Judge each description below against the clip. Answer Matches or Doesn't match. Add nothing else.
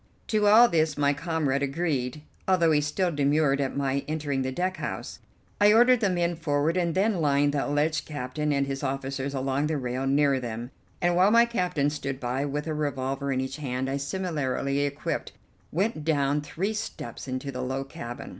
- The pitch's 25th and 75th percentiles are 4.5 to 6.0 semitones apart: Doesn't match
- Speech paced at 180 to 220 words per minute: Matches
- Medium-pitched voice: Matches